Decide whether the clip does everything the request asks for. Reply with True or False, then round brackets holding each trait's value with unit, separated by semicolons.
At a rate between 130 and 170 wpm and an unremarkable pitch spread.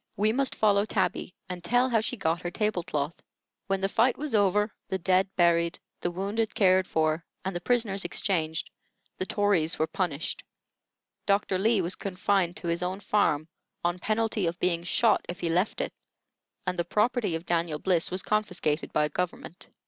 False (180 wpm; 3.5 semitones)